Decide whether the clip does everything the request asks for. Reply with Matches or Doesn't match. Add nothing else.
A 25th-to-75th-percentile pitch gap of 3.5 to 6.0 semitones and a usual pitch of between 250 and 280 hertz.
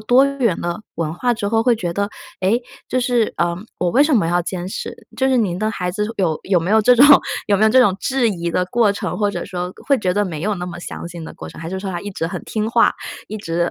Doesn't match